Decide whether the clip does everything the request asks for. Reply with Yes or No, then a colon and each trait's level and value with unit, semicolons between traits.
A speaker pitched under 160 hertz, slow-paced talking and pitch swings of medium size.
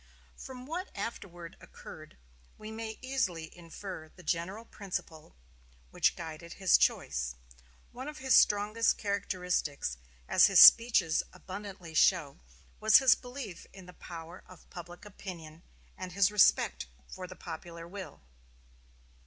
No: medium, 185 Hz; slow, 130 wpm; average, 4.3 semitones